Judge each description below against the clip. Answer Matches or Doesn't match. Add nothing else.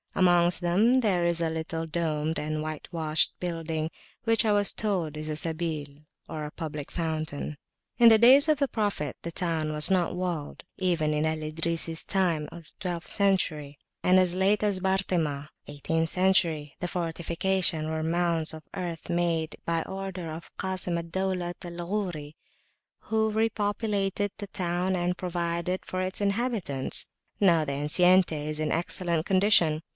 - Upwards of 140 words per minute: Matches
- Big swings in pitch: Doesn't match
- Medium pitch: Matches